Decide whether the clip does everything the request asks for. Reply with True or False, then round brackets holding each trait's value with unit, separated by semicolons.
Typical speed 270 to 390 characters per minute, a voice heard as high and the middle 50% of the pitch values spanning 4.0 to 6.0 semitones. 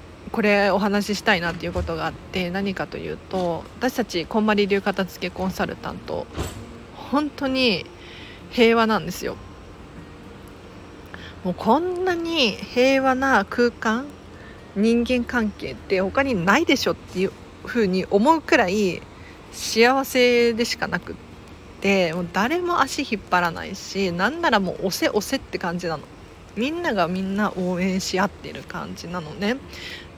True (285 characters per minute; 205 Hz; 5.3 semitones)